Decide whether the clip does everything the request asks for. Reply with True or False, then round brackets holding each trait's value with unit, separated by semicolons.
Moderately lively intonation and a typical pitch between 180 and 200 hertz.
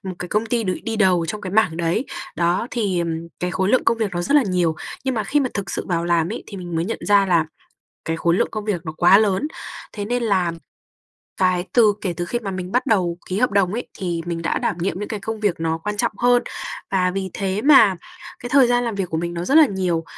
True (4.1 semitones; 190 Hz)